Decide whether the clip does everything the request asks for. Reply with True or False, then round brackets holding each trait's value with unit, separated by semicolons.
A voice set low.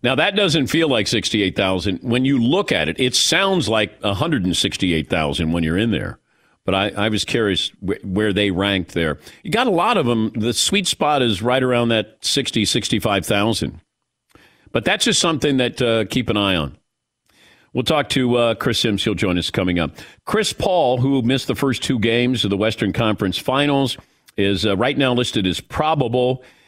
True (115 Hz)